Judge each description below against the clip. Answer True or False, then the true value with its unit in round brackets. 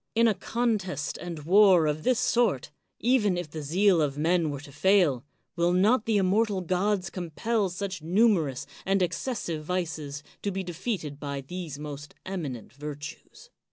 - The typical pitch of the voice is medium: True (180 Hz)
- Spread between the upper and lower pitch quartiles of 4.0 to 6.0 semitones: True (5.0 semitones)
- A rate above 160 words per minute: False (155 wpm)